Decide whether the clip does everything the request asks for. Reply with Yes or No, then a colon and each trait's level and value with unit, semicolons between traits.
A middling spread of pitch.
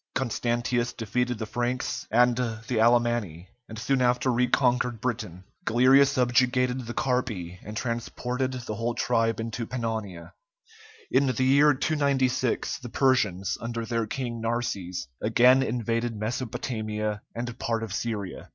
No: narrow, 2.2 semitones